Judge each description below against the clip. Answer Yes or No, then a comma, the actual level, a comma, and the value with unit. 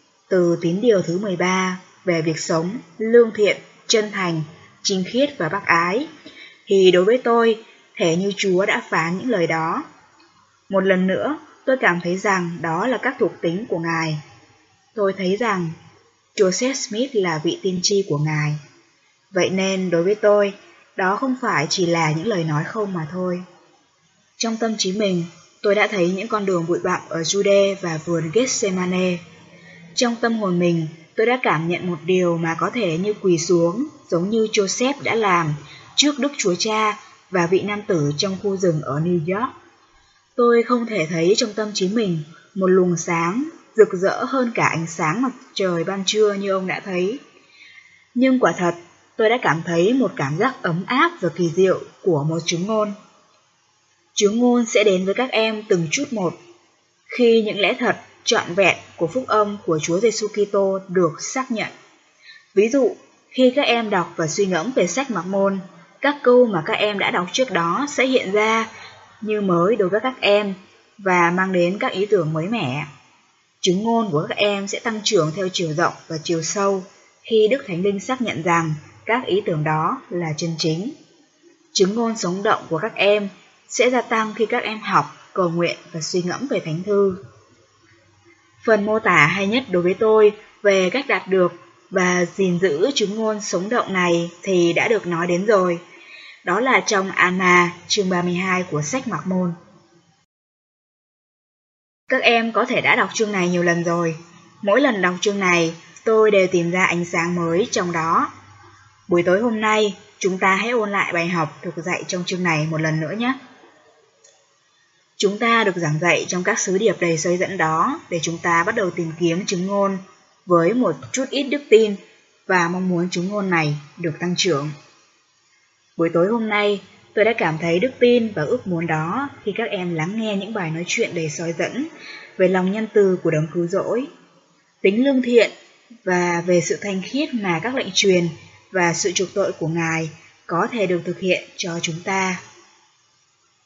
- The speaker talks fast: No, average, 190 wpm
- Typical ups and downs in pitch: Yes, average, 4.1 semitones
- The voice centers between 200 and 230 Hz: No, high, 190 Hz